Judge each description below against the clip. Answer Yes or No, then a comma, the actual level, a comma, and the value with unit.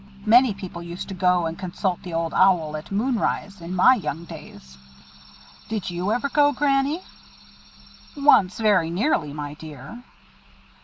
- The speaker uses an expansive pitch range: Yes, wide, 5.8 semitones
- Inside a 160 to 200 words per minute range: No, average, 150 wpm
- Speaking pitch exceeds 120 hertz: Yes, medium, 185 Hz